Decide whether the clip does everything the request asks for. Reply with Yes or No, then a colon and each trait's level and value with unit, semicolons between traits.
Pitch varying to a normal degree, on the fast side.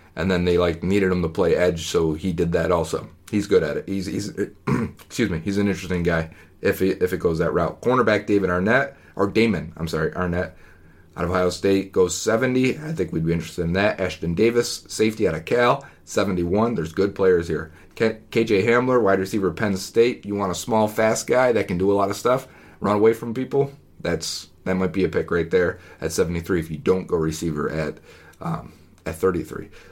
Yes: average, 3.9 semitones; fast, 215 wpm